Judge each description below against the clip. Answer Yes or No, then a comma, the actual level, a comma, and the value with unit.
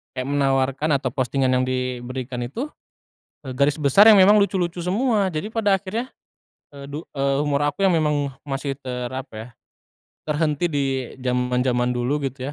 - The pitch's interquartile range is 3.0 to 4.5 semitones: No, average, 4.9 semitones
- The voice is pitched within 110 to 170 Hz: Yes, medium, 140 Hz